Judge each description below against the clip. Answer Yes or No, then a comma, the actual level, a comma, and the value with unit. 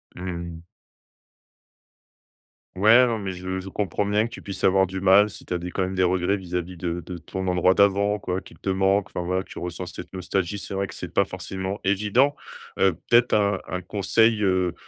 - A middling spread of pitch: No, narrow, 1.9 semitones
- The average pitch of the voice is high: No, very low, 95 Hz